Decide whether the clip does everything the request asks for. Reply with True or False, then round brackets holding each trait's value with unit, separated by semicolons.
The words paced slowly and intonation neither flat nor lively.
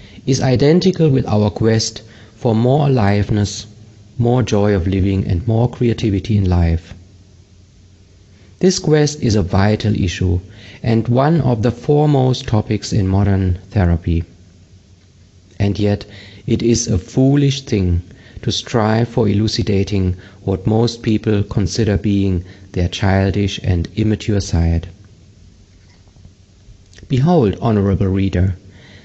True (115 wpm; 3.0 semitones)